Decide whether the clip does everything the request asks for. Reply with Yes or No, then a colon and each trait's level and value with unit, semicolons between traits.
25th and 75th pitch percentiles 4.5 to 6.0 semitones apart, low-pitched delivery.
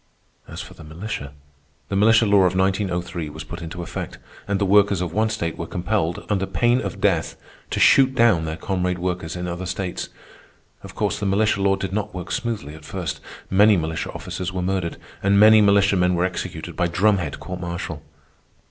No: average, 2.8 semitones; very low, 95 Hz